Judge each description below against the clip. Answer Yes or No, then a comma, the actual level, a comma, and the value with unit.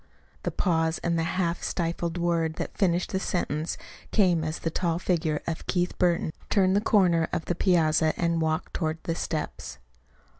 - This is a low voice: No, medium, 170 Hz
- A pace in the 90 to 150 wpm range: No, average, 175 wpm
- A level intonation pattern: Yes, narrow, 1.7 semitones